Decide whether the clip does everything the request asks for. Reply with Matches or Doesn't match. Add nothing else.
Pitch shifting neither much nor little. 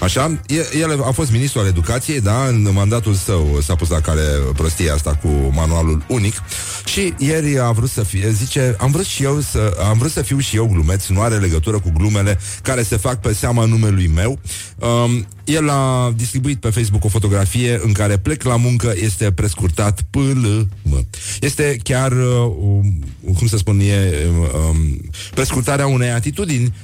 Matches